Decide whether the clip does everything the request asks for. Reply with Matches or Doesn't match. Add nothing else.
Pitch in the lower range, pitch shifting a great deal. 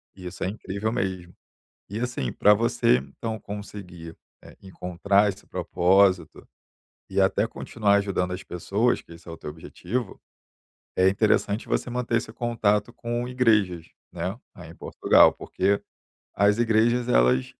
Doesn't match